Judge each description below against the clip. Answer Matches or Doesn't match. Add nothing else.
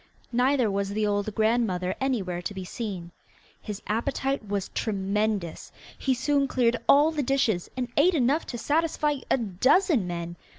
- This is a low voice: Doesn't match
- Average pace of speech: Matches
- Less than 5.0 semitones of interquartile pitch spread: Doesn't match